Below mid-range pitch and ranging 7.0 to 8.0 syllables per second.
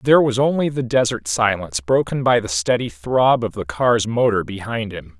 No: low, 115 Hz; 5.1 syllables/s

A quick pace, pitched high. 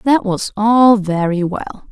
No: average, 155 wpm; high, 210 Hz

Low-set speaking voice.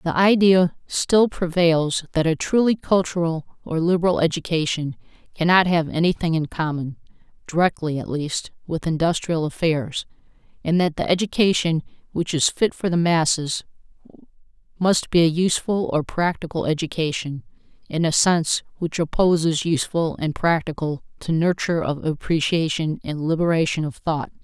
No: medium, 165 Hz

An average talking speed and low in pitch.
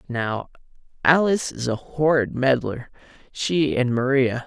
No: slow, 105 wpm; low, 130 Hz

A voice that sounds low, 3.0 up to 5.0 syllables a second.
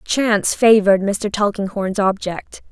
No: high, 205 Hz; 4.3 syllables/s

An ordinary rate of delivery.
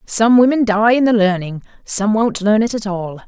No: fast, 220 wpm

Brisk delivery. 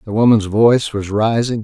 No: average, 185 wpm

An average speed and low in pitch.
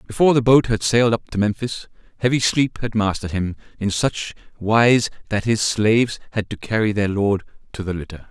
Yes: average, 195 wpm; low, 110 Hz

